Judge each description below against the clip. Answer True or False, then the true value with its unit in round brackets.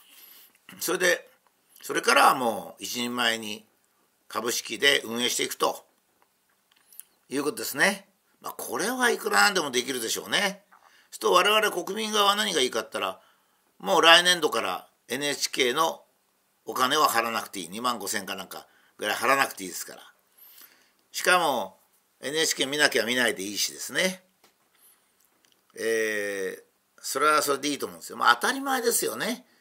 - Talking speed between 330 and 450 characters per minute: False (320 characters per minute)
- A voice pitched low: False (195 Hz)